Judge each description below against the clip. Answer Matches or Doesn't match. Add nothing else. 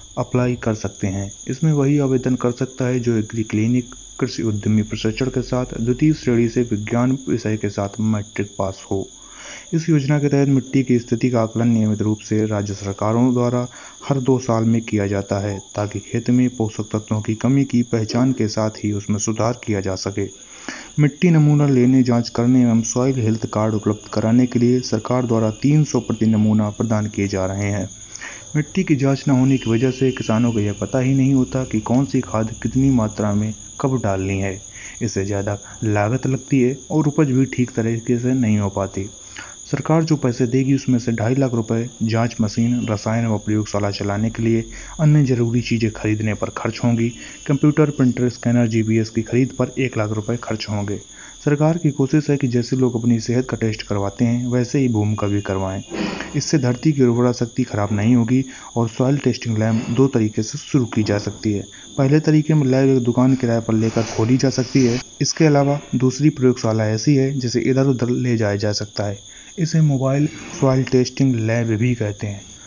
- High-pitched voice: Doesn't match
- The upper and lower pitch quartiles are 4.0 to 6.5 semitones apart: Doesn't match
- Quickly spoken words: Matches